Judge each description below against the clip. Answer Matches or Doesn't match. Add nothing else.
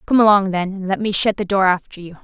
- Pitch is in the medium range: Doesn't match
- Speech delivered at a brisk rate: Matches